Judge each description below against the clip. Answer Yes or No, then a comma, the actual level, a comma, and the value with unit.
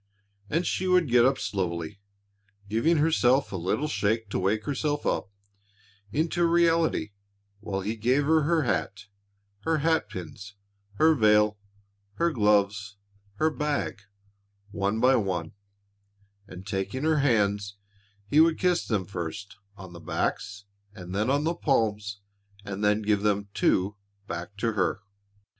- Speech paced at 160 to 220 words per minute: No, average, 140 wpm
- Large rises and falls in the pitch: Yes, wide, 6.7 semitones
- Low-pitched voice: Yes, low, 105 Hz